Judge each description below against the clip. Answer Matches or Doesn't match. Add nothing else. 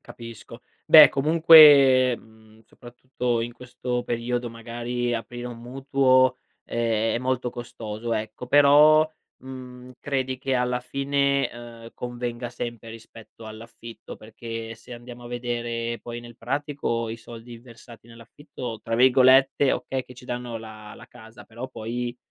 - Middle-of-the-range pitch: Doesn't match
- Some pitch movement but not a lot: Doesn't match